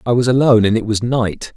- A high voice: No, low, 115 Hz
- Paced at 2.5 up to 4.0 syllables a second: No, 6.3 syllables/s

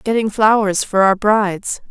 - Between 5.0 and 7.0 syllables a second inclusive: No, 4.4 syllables/s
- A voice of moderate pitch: No, high, 205 Hz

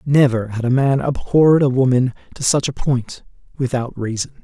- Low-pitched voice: Yes, low, 130 Hz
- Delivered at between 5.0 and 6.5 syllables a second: Yes, 5.1 syllables/s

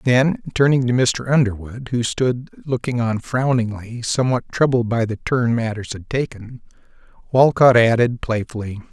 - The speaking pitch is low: Yes, low, 120 Hz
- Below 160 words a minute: Yes, average, 140 wpm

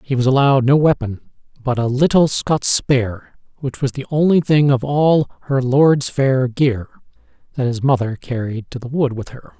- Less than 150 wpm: No, average, 190 wpm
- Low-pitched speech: Yes, low, 130 Hz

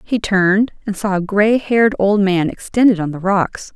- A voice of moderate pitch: No, high, 200 Hz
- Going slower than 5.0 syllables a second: Yes, 4.8 syllables/s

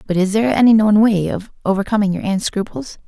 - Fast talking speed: Yes, fast, 215 wpm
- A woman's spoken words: Yes, female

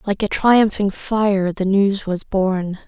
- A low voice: No, high, 200 Hz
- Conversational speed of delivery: Yes, average, 165 wpm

